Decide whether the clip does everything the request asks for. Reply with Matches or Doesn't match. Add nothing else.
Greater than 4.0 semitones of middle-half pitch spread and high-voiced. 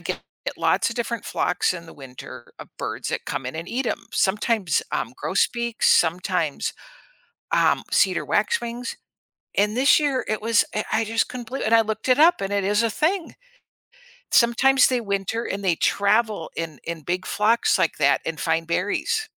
Matches